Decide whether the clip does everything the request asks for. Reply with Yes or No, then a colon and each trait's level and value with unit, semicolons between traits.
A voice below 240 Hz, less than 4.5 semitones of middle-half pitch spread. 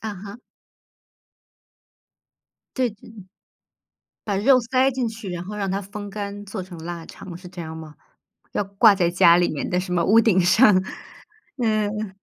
Yes: high, 200 Hz; average, 3.3 semitones